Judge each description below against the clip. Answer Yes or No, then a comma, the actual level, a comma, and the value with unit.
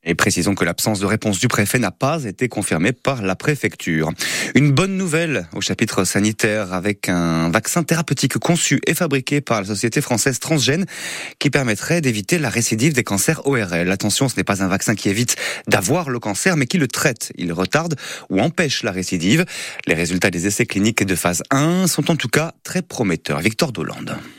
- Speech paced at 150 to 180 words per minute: No, average, 190 wpm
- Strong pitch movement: Yes, wide, 6.1 semitones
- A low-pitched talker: Yes, low, 115 Hz